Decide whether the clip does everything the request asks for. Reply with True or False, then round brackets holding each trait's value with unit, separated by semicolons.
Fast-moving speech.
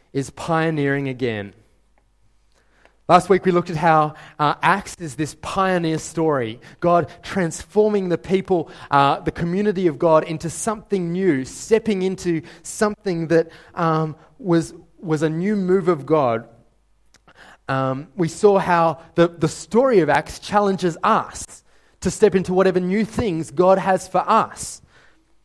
False (140 wpm)